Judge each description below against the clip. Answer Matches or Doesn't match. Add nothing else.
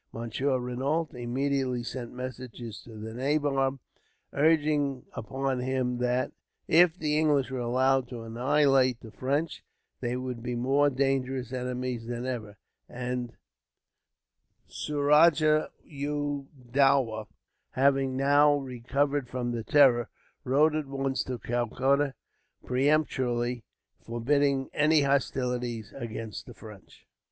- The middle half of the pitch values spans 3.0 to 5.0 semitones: Doesn't match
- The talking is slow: Matches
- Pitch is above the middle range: Doesn't match